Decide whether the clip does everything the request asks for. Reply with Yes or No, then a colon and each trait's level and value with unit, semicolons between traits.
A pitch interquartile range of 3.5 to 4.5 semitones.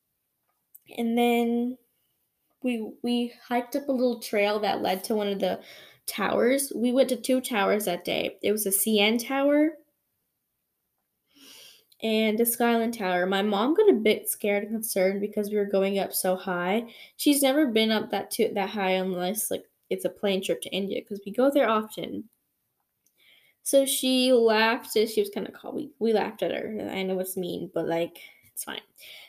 Yes: average, 3.8 semitones